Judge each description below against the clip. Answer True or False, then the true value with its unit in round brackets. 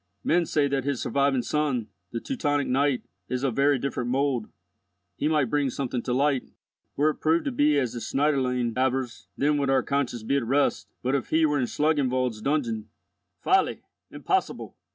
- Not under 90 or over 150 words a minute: False (180 wpm)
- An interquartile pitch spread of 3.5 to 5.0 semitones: False (2.6 semitones)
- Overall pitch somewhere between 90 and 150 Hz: True (140 Hz)